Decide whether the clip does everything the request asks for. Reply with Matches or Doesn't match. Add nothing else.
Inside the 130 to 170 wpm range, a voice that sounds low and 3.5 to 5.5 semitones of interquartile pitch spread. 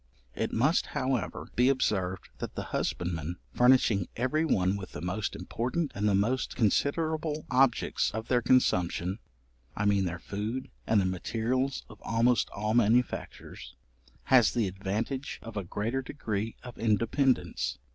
Matches